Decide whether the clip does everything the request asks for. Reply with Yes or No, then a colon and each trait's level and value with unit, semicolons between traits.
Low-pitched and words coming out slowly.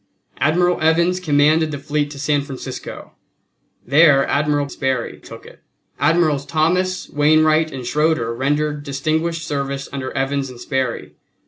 No: medium, 145 Hz; slow, 130 wpm